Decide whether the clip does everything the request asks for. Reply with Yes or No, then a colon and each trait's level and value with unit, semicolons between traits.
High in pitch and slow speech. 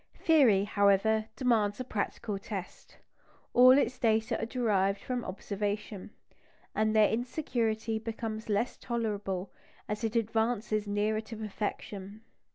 Yes: high, 220 Hz; slow, 120 wpm